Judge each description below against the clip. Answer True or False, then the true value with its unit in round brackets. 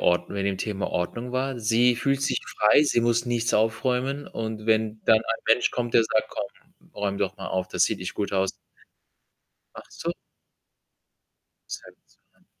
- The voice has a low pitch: True (115 Hz)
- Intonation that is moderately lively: True (3.2 semitones)